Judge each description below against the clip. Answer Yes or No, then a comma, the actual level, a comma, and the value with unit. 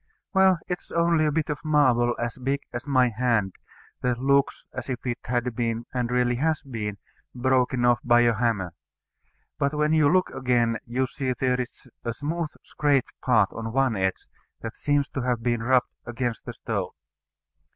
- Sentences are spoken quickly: No, average, 180 wpm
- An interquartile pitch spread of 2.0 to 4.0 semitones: Yes, average, 2.9 semitones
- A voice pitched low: Yes, low, 125 Hz